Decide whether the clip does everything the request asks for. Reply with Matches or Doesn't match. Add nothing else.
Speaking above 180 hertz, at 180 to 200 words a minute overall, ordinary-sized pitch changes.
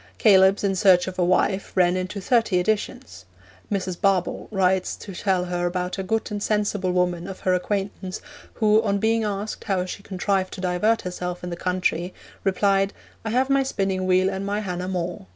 Doesn't match